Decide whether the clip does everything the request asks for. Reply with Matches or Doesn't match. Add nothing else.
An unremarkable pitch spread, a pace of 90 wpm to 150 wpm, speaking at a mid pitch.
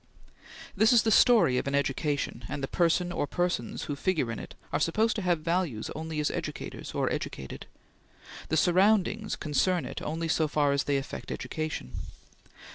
Doesn't match